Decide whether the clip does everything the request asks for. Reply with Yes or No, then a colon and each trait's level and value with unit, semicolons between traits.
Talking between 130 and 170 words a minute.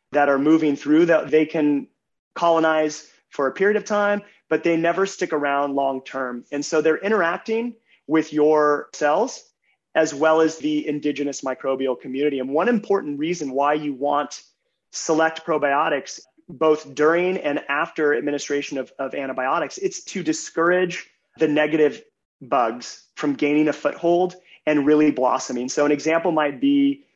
Yes: average, 150 wpm